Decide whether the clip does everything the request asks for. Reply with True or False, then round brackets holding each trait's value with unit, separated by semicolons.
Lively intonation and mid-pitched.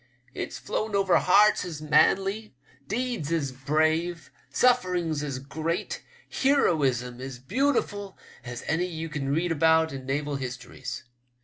True (5.9 semitones; 160 Hz)